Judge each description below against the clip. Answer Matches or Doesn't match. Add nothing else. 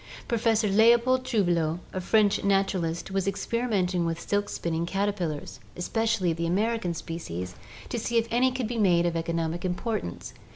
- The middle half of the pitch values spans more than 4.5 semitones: Matches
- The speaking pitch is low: Doesn't match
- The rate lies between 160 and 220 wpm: Doesn't match